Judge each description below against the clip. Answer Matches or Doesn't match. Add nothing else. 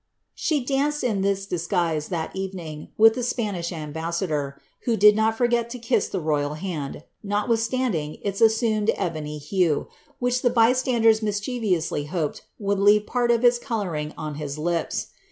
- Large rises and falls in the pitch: Matches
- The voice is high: Matches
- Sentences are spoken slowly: Doesn't match